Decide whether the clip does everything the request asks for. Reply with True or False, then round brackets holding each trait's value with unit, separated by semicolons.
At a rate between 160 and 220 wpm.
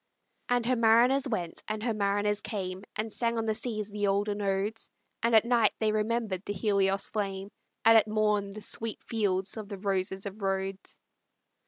True (180 wpm)